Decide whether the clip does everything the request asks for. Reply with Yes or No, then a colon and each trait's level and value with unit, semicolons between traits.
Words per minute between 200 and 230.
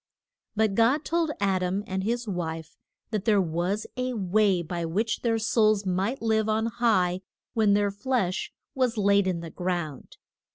No: average, 165 wpm